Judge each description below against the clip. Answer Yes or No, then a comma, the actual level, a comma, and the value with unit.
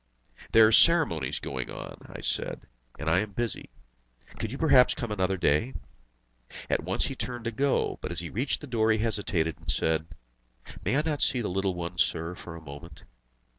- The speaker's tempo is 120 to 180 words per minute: No, average, 195 wpm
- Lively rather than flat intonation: Yes, wide, 6.5 semitones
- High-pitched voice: No, low, 100 Hz